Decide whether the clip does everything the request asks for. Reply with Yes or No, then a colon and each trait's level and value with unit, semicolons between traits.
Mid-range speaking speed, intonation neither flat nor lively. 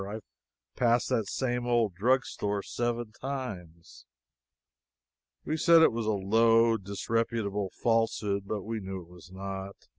No: slow, 130 wpm; average, 3.3 semitones